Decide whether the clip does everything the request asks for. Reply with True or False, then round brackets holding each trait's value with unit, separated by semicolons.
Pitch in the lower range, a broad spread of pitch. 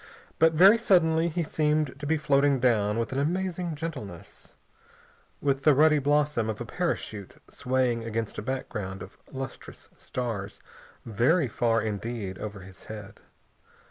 True (130 Hz; 6.0 semitones)